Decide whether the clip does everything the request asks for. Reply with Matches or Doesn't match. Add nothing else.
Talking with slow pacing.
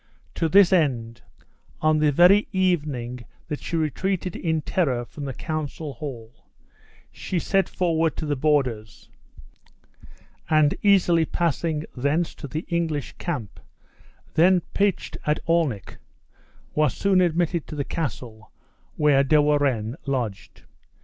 Matches